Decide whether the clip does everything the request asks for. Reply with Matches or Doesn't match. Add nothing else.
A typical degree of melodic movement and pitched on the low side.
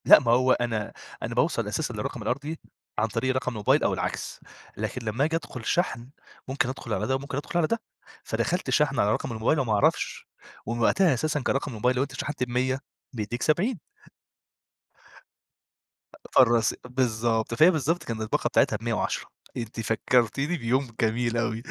Matches